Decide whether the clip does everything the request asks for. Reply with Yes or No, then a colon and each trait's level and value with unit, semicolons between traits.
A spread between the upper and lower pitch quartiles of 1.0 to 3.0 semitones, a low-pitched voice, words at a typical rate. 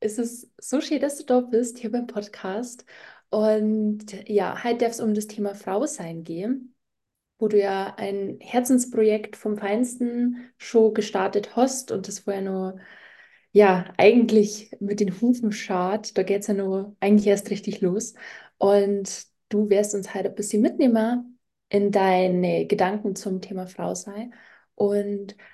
No: average, 2.7 semitones; high, 210 Hz; average, 160 wpm